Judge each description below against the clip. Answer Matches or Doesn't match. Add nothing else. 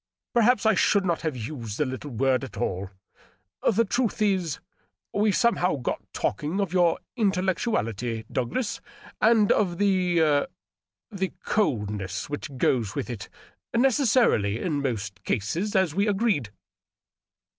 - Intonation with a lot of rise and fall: Matches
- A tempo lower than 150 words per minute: Matches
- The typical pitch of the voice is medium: Matches